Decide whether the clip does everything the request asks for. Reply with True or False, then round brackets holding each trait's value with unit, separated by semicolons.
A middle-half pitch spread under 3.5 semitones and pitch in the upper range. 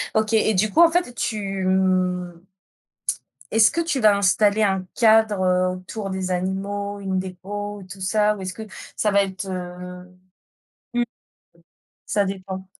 True (2.4 semitones; 195 Hz)